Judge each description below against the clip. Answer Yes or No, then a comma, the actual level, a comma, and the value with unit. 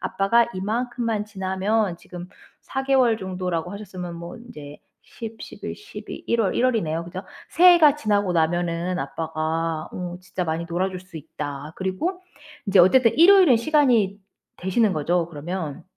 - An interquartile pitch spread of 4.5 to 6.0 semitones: Yes, average, 5.2 semitones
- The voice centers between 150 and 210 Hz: Yes, high, 190 Hz